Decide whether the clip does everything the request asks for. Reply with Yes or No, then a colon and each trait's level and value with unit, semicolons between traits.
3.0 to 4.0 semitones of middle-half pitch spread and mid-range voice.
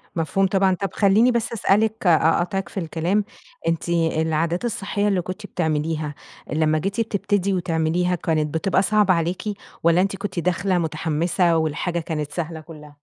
Yes: average, 3.3 semitones; medium, 175 Hz